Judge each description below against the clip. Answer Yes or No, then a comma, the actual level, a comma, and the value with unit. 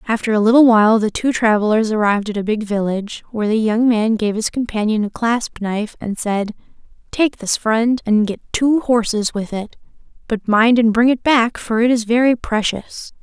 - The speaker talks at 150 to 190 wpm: No, average, 200 wpm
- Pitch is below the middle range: No, high, 225 Hz